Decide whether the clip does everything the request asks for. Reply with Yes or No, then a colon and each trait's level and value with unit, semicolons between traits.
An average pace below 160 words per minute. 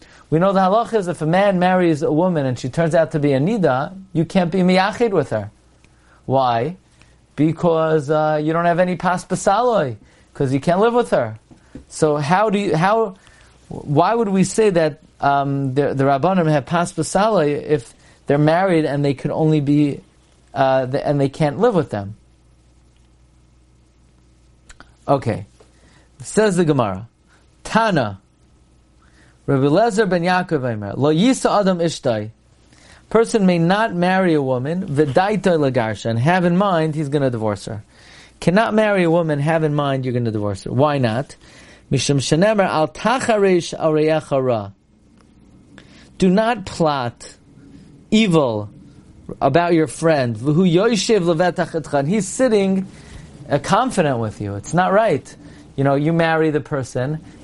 Yes: average, 145 wpm